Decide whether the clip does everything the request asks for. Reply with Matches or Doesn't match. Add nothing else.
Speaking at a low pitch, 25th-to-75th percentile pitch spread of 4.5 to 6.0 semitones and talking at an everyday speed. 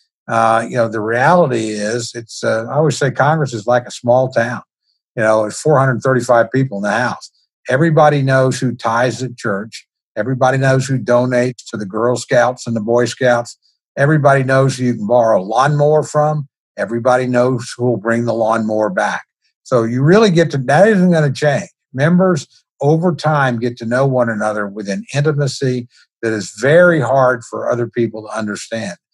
Doesn't match